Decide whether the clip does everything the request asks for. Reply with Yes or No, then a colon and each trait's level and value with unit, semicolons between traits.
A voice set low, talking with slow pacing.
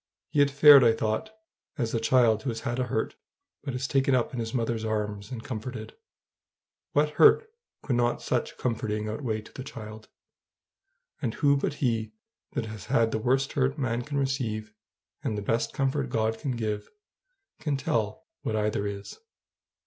No: low, 115 Hz; average, 175 wpm